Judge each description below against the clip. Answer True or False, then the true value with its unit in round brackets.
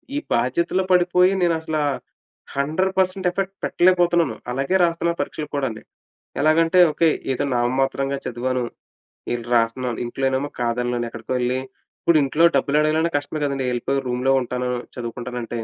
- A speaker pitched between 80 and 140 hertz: True (135 Hz)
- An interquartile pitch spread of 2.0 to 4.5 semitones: False (5.3 semitones)